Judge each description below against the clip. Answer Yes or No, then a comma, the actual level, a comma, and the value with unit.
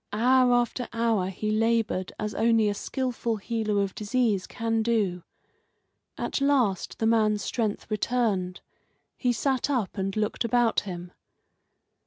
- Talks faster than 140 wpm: No, slow, 135 wpm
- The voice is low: No, high, 225 Hz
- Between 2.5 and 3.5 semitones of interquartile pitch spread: Yes, average, 2.8 semitones